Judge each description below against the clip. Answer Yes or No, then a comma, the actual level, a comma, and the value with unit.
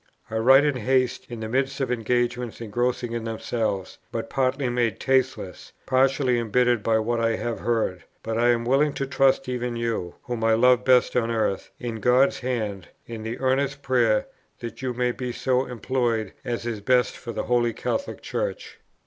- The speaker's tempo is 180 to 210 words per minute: Yes, average, 185 wpm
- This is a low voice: Yes, low, 120 Hz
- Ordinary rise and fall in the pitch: No, narrow, 2.2 semitones